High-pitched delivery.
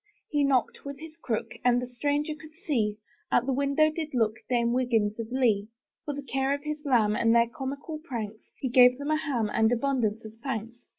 Yes: very high, 255 Hz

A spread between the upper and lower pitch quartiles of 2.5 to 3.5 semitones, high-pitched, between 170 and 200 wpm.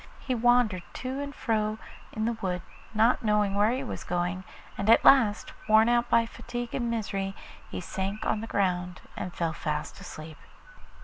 No: average, 3.9 semitones; high, 215 Hz; average, 175 wpm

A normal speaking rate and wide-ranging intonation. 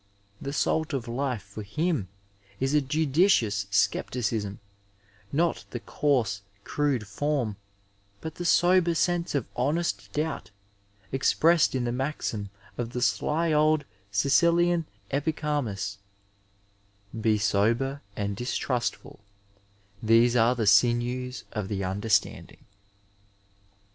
No: slow, 115 wpm; wide, 6.0 semitones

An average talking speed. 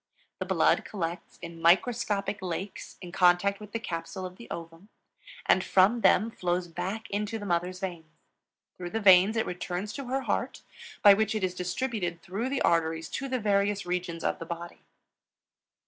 Yes: average, 175 wpm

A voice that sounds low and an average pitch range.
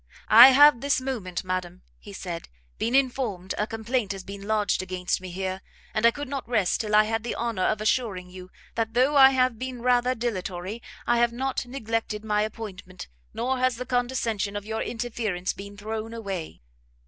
No: high, 220 Hz; average, 4.0 semitones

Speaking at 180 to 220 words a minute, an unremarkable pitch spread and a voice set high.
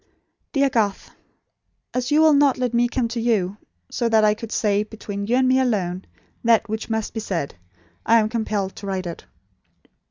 Yes: average, 190 wpm; average, 3.2 semitones; high, 220 Hz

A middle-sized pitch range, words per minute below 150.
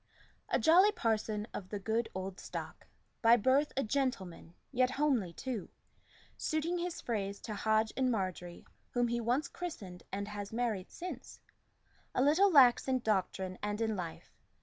No: average, 5.0 semitones; average, 155 wpm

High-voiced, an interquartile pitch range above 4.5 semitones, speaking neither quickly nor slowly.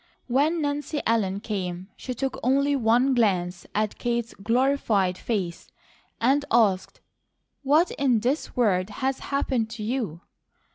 No: high, 235 Hz; average, 5.0 semitones; slow, 130 wpm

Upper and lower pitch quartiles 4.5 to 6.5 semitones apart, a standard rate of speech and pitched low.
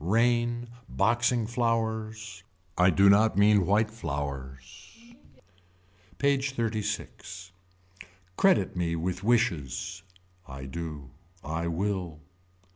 No: wide, 5.6 semitones; slow, 90 wpm; low, 100 Hz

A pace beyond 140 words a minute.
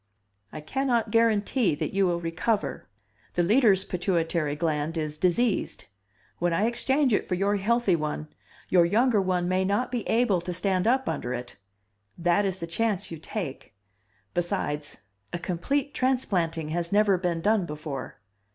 Yes: average, 160 wpm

